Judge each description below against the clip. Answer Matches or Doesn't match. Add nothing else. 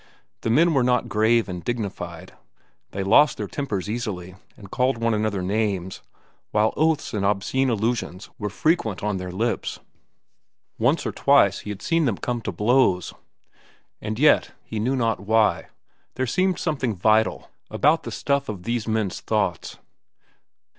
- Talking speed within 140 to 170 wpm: Matches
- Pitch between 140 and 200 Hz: Doesn't match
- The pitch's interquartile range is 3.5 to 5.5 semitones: Matches